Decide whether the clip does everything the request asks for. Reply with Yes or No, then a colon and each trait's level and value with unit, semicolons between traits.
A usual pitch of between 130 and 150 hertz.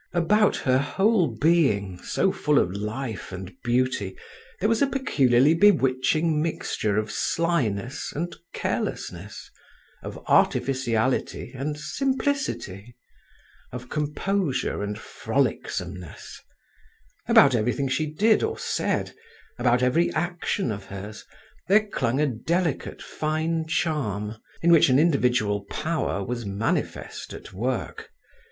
Yes: low, 135 Hz